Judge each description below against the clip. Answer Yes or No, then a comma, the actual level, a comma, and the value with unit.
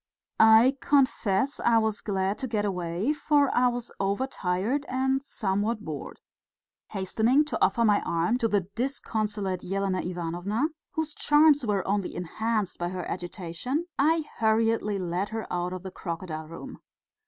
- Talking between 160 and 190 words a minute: No, average, 145 wpm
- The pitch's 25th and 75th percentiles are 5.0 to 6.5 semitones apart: Yes, average, 5.3 semitones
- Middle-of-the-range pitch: No, high, 210 Hz